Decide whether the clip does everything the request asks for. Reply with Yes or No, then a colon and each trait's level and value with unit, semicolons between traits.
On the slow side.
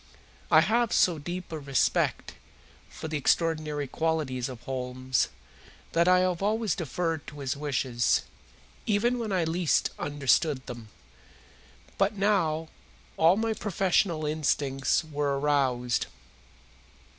Yes: slow, 120 wpm